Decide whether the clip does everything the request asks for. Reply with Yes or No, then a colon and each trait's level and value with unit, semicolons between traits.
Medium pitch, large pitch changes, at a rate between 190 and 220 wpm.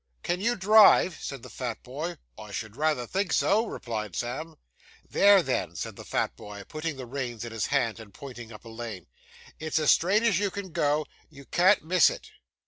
Yes: medium, 145 Hz; wide, 7.4 semitones; average, 200 wpm